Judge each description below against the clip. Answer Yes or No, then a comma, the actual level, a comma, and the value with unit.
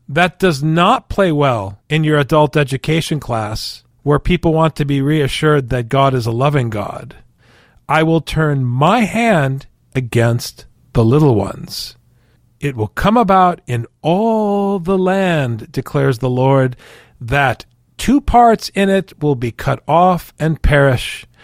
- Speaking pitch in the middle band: Yes, medium, 145 Hz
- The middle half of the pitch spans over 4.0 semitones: Yes, average, 5.3 semitones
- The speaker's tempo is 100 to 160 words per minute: Yes, average, 150 wpm